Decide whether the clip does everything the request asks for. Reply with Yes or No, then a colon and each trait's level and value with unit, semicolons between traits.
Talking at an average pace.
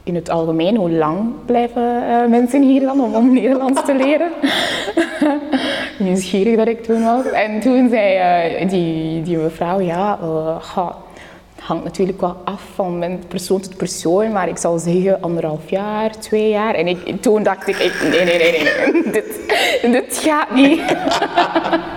Yes: average, 170 wpm